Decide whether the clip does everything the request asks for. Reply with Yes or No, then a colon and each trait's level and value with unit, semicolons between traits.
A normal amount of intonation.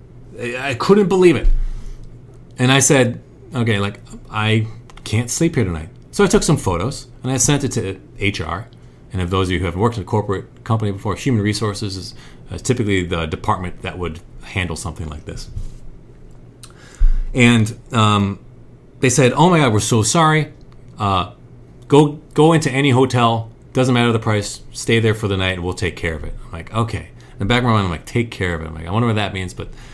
Yes: average, 4.4 semitones